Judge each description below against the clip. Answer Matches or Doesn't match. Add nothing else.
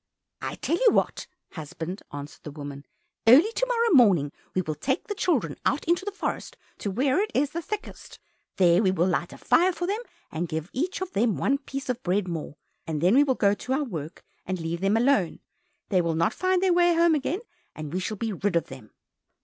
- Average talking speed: Doesn't match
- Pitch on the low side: Doesn't match